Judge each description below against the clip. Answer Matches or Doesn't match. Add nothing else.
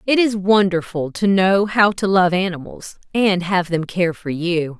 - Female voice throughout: Matches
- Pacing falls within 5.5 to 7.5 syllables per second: Doesn't match